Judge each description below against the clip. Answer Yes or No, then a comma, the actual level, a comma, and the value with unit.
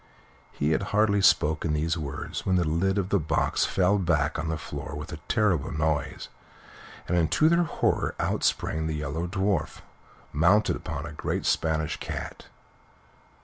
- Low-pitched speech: Yes, very low, 80 Hz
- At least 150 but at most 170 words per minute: Yes, average, 160 wpm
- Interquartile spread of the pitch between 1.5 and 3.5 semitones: No, average, 3.9 semitones